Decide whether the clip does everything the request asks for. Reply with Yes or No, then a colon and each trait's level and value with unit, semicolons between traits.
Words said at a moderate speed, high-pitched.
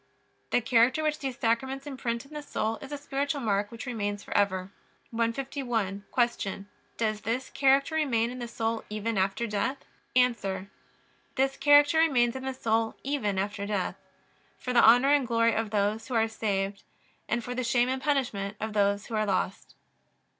Yes: average, 170 wpm; high, 230 Hz